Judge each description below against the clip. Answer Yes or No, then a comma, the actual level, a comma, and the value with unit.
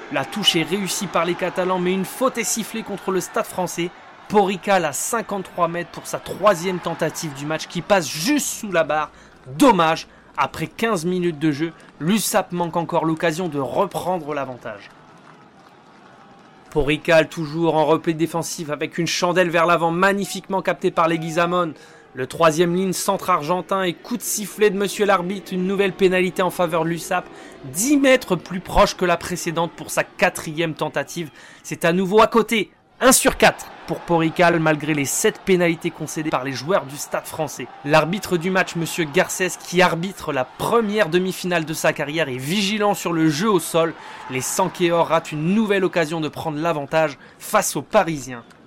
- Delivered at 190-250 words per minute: No, average, 175 wpm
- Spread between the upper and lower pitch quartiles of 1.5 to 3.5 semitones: Yes, average, 3.1 semitones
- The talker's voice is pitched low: No, medium, 175 Hz